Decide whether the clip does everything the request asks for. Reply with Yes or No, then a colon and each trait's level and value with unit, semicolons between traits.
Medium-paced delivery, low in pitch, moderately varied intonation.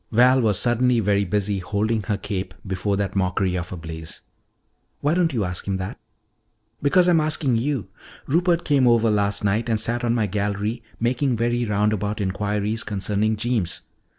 Yes: average, 170 wpm; low, 105 Hz; average, 3.3 semitones